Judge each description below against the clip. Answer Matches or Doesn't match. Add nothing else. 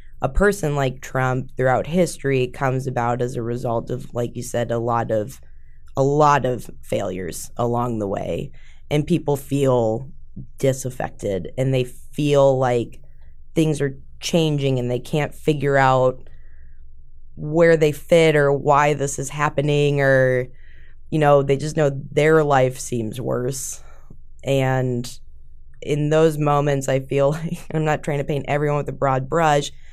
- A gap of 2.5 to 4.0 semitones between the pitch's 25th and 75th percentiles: Matches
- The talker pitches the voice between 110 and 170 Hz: Matches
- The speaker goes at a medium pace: Matches